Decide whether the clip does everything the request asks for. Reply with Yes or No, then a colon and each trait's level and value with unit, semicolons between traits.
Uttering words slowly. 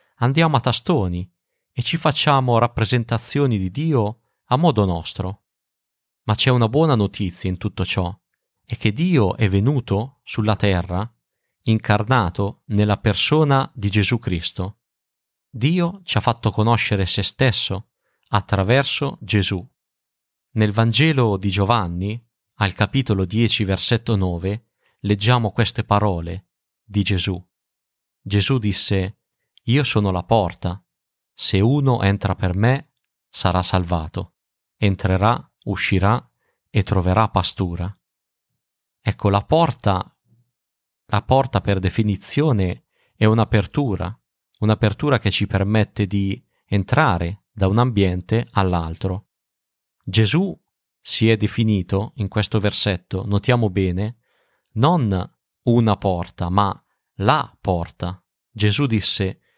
Yes: slow, 110 wpm